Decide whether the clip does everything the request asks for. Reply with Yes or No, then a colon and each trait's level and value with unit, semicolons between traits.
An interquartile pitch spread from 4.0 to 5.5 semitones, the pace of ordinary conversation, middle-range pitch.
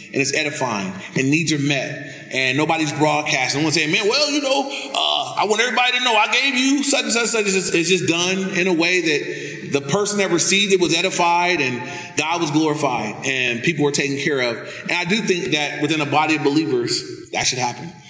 No: average, 5.1 semitones; fast, 235 wpm; medium, 170 Hz